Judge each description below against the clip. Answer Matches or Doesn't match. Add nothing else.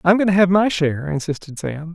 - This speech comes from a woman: Doesn't match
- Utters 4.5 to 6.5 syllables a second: Matches